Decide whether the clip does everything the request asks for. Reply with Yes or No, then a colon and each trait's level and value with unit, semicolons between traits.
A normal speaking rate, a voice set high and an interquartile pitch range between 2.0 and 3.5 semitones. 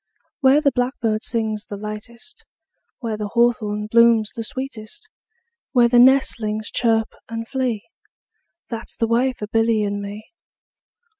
Yes: average, 145 wpm; high, 230 Hz; narrow, 2.4 semitones